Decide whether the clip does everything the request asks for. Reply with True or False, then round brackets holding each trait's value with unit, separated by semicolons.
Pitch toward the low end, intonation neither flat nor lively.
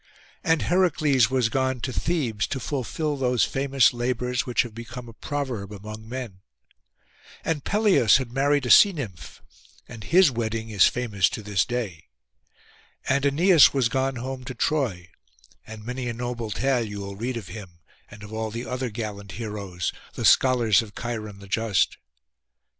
True (120 Hz; 3.8 semitones)